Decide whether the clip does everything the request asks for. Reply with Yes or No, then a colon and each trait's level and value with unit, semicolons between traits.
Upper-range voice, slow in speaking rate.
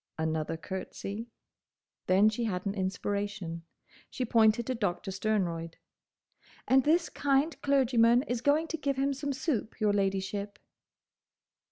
Yes: high, 215 Hz; slow, 130 wpm